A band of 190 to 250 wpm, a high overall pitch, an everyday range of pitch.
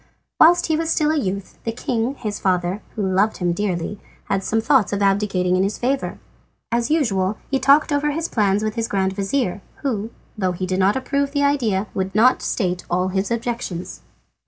No: average, 195 wpm; high, 210 Hz; wide, 5.7 semitones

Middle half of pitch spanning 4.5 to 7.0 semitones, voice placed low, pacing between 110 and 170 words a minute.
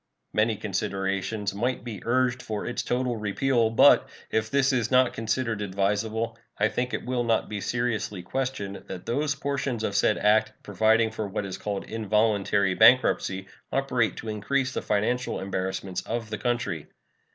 No: average, 3.2 semitones; low, 110 Hz; average, 160 wpm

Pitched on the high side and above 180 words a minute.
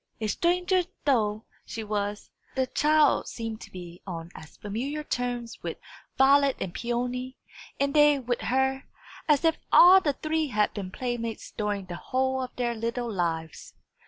No: high, 245 Hz; average, 160 wpm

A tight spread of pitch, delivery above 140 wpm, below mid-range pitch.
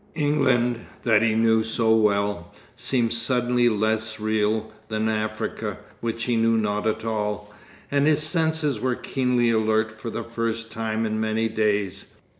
Yes: narrow, 1.7 semitones; average, 150 wpm; low, 110 Hz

